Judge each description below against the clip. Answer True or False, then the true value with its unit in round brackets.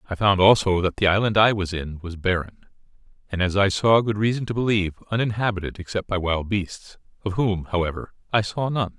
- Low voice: True (100 Hz)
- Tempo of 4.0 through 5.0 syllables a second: False (5.6 syllables/s)